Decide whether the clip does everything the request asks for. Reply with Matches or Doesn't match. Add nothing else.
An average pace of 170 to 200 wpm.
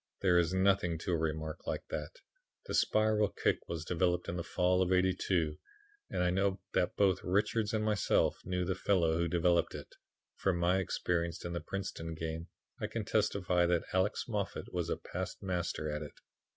Matches